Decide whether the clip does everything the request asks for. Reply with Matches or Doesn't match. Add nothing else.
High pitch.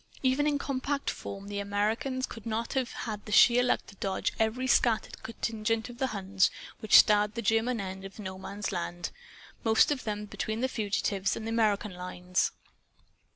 Matches